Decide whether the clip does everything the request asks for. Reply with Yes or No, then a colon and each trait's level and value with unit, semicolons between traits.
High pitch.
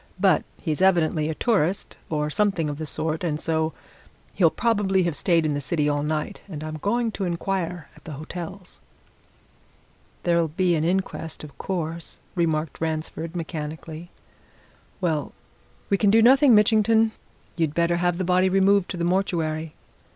No: medium, 170 Hz